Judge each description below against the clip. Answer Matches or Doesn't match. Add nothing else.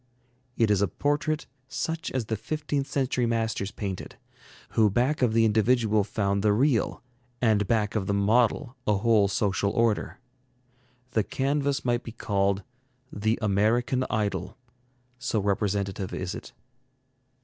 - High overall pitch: Doesn't match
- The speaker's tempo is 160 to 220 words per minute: Doesn't match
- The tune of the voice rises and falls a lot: Doesn't match